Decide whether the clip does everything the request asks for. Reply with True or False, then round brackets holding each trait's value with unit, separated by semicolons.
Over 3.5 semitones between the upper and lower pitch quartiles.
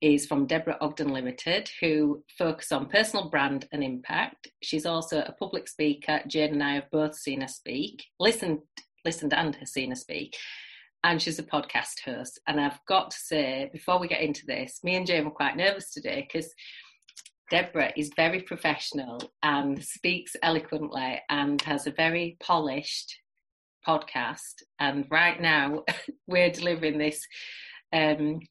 False (2.7 semitones)